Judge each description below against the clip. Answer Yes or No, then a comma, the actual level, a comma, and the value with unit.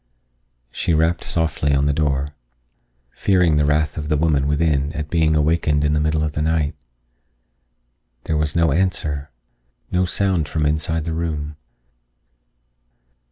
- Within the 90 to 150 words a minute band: Yes, average, 145 wpm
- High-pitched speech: No, very low, 75 Hz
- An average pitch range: No, narrow, 1.8 semitones